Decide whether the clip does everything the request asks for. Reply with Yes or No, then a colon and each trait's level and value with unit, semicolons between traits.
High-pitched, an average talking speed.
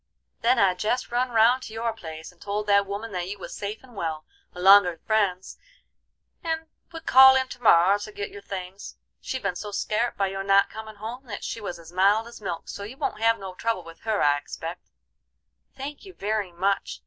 No: high, 205 Hz; fast, 210 wpm